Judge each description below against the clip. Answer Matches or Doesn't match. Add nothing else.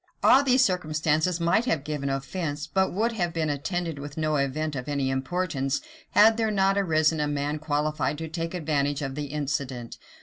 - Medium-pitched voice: Matches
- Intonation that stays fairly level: Doesn't match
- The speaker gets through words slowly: Doesn't match